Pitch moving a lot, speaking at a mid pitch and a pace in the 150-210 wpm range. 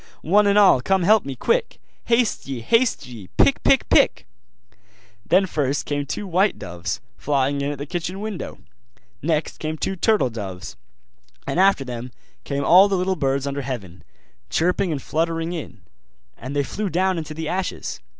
Yes: wide, 5.8 semitones; medium, 160 Hz; average, 170 wpm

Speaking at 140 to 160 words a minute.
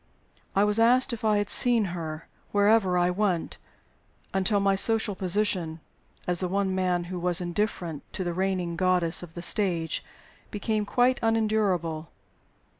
Yes: average, 150 wpm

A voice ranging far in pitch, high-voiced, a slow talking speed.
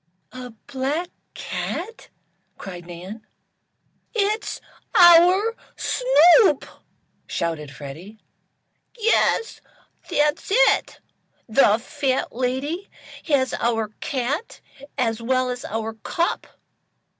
Yes: wide, 7.8 semitones; very high, 260 Hz; slow, 85 wpm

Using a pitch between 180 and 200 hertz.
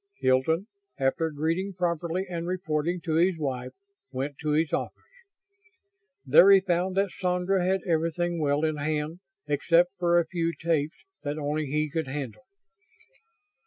No: medium, 165 Hz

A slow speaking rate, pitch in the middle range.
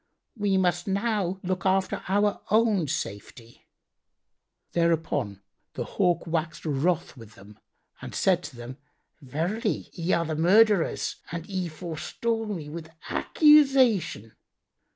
Yes: slow, 120 wpm; medium, 175 Hz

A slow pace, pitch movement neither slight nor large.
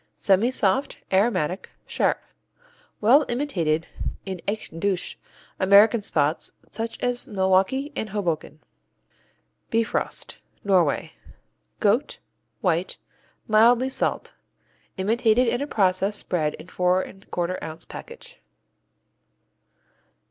Yes: slow, 90 wpm; average, 4.3 semitones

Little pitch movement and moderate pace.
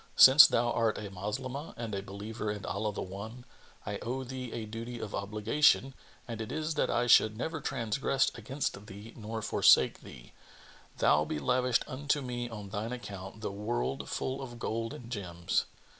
No: average, 3.6 semitones; average, 175 wpm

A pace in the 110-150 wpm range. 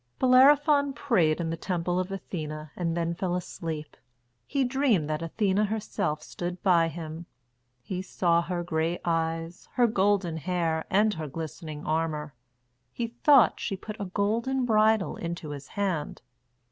Yes: average, 145 wpm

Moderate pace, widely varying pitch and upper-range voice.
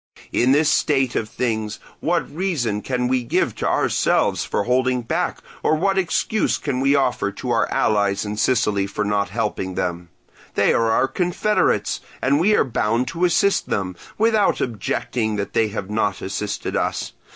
No: average, 170 wpm; wide, 5.7 semitones; low, 120 Hz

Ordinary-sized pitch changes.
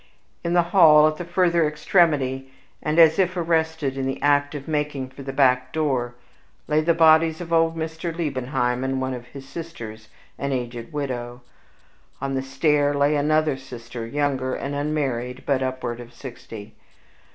Yes: average, 3.5 semitones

